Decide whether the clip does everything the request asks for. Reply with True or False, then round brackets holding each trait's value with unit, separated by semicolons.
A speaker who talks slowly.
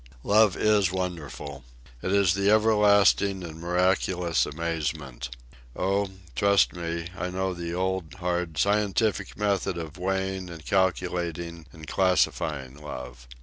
True (120 wpm)